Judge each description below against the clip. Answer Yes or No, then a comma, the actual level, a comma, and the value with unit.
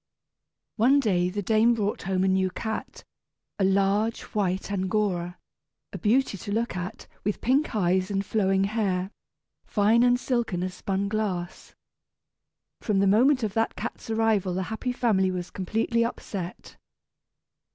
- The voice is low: No, high, 200 Hz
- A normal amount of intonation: Yes, average, 3.0 semitones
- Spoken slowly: No, average, 145 wpm